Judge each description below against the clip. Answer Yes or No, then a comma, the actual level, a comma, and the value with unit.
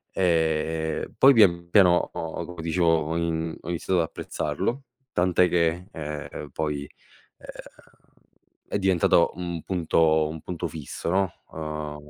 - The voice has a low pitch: Yes, very low, 85 Hz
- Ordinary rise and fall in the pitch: No, narrow, 2.1 semitones